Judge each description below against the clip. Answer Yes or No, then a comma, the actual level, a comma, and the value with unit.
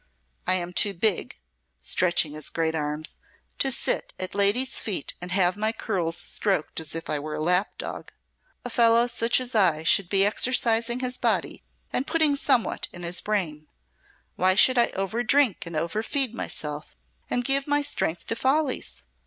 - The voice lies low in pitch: No, high, 200 Hz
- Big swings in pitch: Yes, wide, 6.4 semitones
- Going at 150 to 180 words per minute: Yes, average, 170 wpm